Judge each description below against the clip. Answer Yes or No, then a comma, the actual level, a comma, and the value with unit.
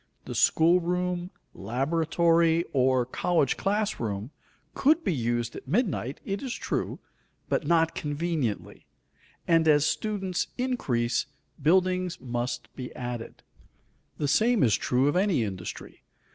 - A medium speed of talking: No, slow, 125 wpm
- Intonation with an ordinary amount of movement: No, wide, 6.5 semitones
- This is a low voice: No, medium, 160 Hz